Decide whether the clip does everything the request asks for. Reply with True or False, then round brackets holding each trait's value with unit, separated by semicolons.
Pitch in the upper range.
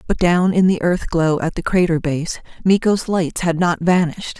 False (175 Hz)